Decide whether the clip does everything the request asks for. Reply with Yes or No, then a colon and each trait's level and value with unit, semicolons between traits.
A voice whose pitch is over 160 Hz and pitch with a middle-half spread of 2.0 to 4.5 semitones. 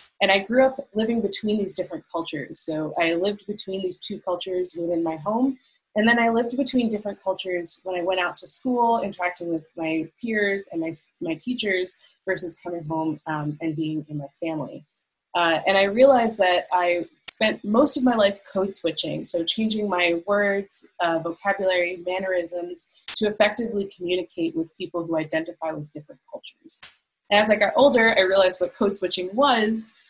Yes: medium, 185 Hz; average, 3.8 semitones